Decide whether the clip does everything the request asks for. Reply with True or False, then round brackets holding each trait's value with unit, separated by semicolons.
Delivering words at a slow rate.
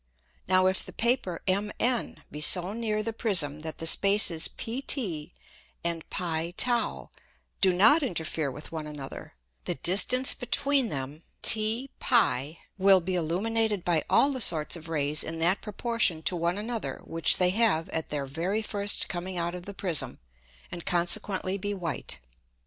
False (160 wpm)